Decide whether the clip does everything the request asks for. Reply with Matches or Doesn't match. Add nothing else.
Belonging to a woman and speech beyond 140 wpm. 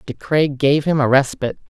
Matches